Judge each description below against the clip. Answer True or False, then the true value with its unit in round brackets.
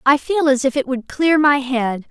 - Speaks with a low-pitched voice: False (275 Hz)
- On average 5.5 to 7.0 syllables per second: False (4.5 syllables/s)